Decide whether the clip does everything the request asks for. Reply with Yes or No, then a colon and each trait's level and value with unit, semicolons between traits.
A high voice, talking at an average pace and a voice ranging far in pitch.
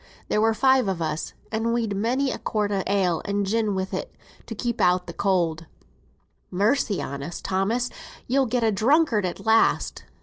No: high, 210 Hz; average, 175 wpm; average, 3.8 semitones